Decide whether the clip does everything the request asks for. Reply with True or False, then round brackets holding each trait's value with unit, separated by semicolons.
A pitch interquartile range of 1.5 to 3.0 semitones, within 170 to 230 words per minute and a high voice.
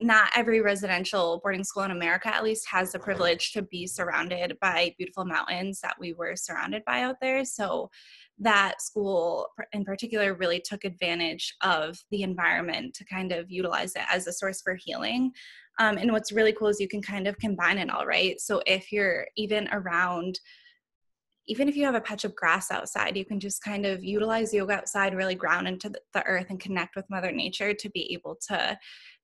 True (2.7 semitones; 195 wpm; 195 Hz)